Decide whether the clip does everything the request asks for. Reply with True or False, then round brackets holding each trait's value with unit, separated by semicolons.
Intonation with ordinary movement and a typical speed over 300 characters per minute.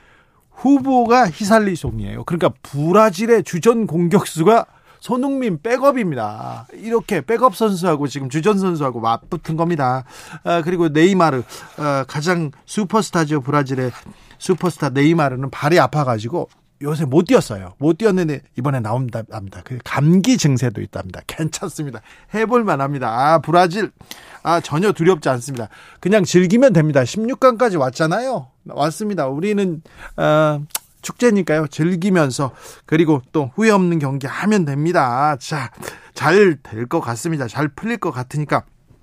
False (6.3 semitones; 320 characters per minute)